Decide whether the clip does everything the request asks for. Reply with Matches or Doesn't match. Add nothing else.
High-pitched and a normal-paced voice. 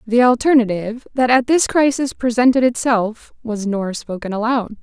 Matches